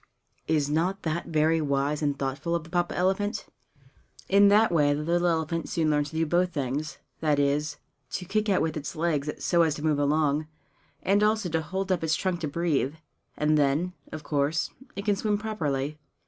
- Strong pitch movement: No, average, 3.3 semitones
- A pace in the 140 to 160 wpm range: No, average, 195 wpm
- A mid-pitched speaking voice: Yes, medium, 160 Hz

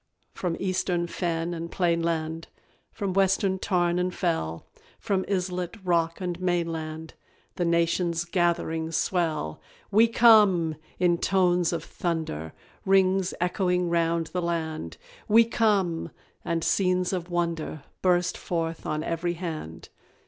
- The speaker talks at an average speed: No, slow, 120 wpm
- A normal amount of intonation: No, narrow, 1.8 semitones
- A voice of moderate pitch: Yes, medium, 175 Hz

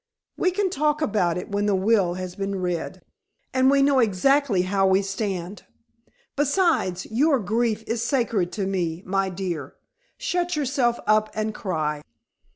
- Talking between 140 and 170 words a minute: Yes, average, 155 wpm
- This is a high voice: Yes, high, 210 Hz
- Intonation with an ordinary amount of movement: No, wide, 6.3 semitones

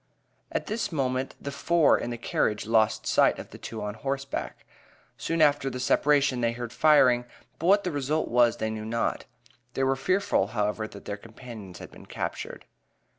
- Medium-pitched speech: No, low, 125 Hz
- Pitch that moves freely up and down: No, average, 4.5 semitones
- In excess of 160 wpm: Yes, average, 180 wpm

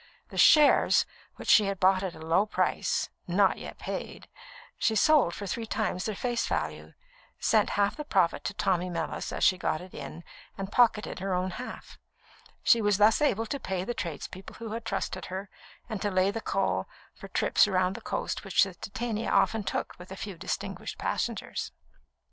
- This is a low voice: No, high, 195 Hz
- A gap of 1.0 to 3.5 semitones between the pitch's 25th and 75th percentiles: Yes, average, 3.2 semitones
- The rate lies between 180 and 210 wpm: Yes, average, 190 wpm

